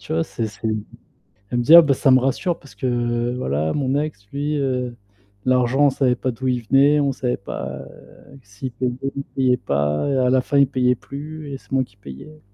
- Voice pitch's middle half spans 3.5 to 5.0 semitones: No, narrow, 2.5 semitones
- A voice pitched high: No, low, 130 Hz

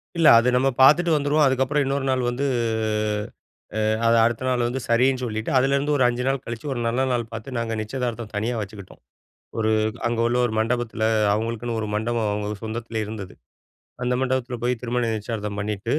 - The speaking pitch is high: No, low, 120 Hz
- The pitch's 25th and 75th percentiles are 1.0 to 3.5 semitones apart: Yes, average, 2.8 semitones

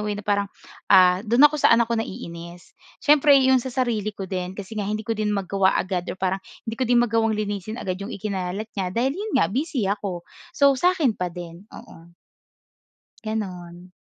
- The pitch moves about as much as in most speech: Yes, average, 4.1 semitones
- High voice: Yes, high, 205 Hz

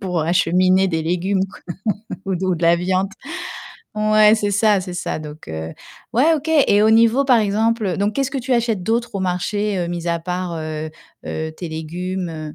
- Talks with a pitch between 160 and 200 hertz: Yes, medium, 185 Hz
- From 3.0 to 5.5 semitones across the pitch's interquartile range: Yes, average, 3.9 semitones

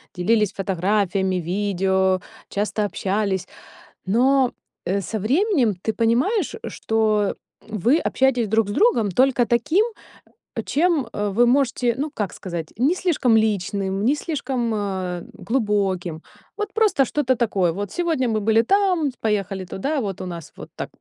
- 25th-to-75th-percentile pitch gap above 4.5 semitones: Yes, wide, 5.5 semitones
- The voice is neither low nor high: No, high, 220 Hz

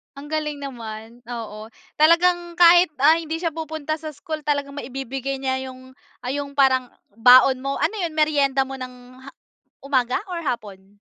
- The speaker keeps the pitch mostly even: No, average, 3.4 semitones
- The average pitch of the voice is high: Yes, very high, 275 Hz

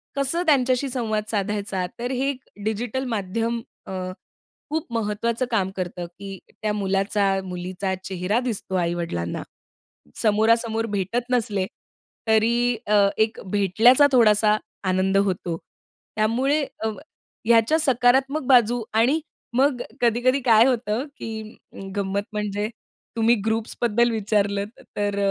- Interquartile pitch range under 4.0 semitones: Yes, average, 3.5 semitones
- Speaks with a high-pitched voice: Yes, high, 220 Hz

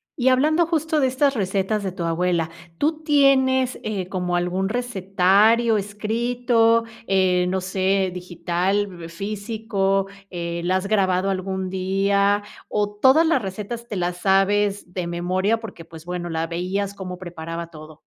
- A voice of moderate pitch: No, high, 195 Hz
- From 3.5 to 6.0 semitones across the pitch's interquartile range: Yes, average, 3.8 semitones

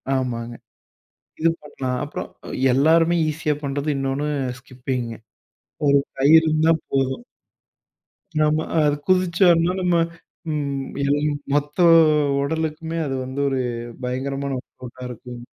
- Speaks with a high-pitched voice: No, medium, 140 Hz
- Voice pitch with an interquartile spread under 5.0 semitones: Yes, average, 3.3 semitones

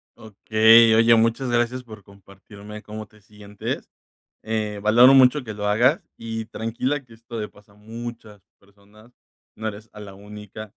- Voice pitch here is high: No, low, 110 Hz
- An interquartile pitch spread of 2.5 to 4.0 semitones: No, narrow, 2.0 semitones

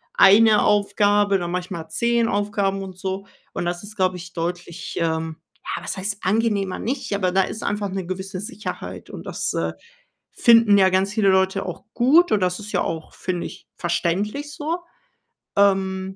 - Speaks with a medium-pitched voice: No, high, 195 Hz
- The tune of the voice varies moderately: No, narrow, 2.3 semitones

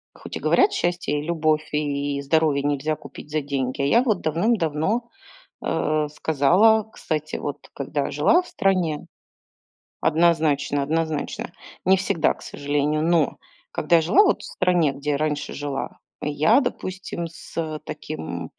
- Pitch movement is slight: No, average, 3.0 semitones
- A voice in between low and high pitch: Yes, medium, 155 Hz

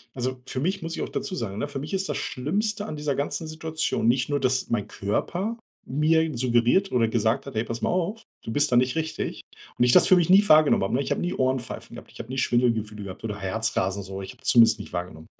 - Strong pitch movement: Yes, wide, 6.0 semitones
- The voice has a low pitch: Yes, low, 130 Hz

